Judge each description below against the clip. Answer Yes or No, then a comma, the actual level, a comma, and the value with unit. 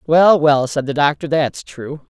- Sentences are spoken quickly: No, average, 195 wpm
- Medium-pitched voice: Yes, medium, 150 Hz